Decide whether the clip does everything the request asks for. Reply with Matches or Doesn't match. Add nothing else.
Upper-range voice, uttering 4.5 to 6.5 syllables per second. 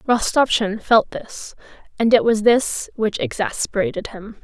Doesn't match